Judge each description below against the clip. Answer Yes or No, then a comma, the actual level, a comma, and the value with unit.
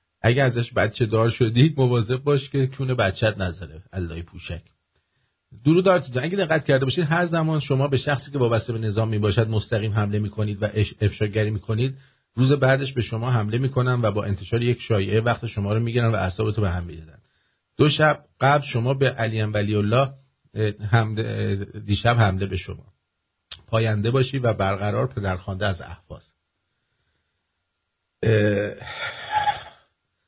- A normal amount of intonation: Yes, average, 4.4 semitones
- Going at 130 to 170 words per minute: Yes, average, 155 wpm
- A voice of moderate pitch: No, low, 110 Hz